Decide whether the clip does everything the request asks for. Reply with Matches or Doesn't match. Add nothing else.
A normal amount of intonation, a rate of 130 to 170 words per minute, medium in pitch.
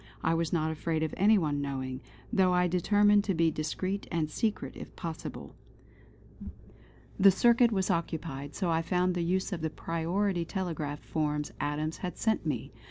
Matches